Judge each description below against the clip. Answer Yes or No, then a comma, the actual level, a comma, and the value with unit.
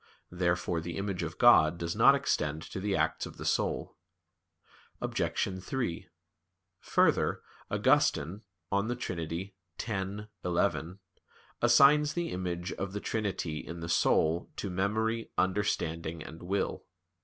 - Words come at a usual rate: No, slow, 125 wpm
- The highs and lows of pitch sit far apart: No, average, 3.5 semitones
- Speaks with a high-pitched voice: No, very low, 95 Hz